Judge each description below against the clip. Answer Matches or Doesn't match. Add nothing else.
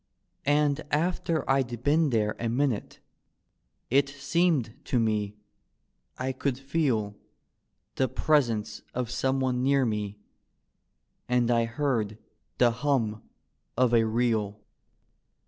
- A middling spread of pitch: Matches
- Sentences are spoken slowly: Matches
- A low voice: Matches